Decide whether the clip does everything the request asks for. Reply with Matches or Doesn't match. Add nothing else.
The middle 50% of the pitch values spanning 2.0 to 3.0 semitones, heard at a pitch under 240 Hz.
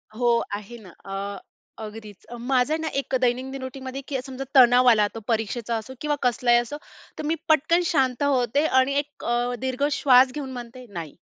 Doesn't match